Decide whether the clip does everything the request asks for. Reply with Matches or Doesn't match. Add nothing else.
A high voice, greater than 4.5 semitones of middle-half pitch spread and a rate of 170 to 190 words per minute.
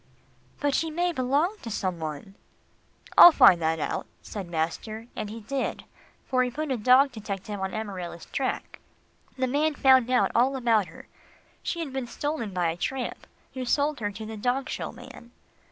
Matches